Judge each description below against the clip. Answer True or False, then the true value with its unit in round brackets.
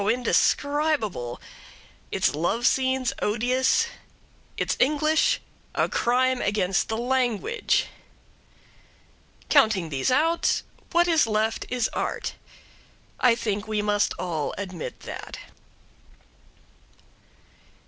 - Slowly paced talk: True (90 wpm)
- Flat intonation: False (4.2 semitones)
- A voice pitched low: False (240 Hz)